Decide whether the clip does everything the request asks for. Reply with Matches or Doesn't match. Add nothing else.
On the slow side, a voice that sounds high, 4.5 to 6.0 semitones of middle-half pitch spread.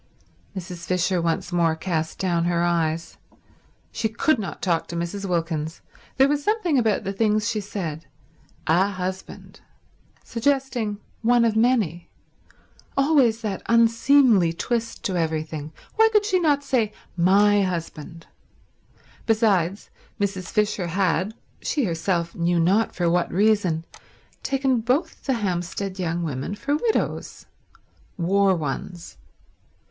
Matches